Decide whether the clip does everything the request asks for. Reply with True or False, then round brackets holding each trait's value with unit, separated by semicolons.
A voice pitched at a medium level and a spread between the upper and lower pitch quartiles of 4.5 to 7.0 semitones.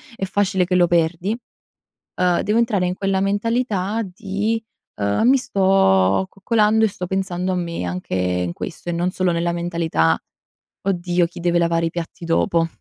False (180 Hz; 2.9 semitones)